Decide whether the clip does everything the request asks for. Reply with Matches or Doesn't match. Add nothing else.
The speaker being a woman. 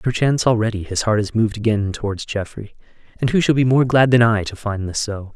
Doesn't match